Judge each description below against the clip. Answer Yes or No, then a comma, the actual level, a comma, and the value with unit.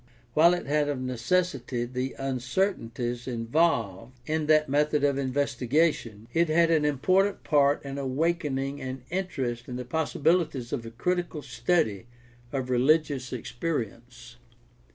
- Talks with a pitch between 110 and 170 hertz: Yes, low, 135 Hz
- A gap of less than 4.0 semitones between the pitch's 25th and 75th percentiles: No, average, 4.3 semitones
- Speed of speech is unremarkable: No, slow, 130 wpm